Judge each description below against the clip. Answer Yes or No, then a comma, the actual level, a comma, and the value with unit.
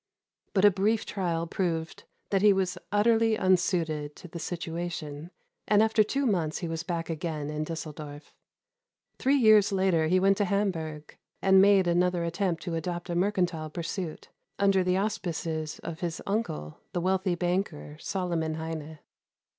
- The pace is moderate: Yes, average, 155 wpm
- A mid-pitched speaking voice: Yes, medium, 175 Hz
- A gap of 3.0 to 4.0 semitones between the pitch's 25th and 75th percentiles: Yes, average, 3.3 semitones